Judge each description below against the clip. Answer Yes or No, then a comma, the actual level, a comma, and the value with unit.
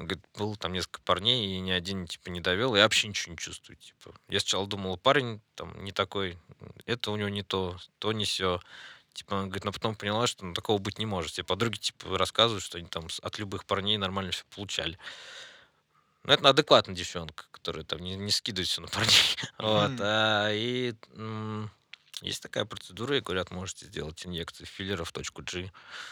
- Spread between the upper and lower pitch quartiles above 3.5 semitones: No, average, 2.8 semitones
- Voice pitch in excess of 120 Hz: No, low, 100 Hz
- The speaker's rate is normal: No, fast, 195 wpm